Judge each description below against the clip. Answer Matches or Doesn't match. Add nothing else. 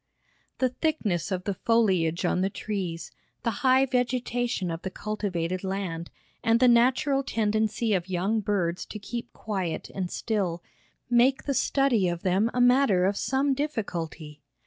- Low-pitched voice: Doesn't match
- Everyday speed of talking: Matches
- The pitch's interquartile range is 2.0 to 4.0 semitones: Doesn't match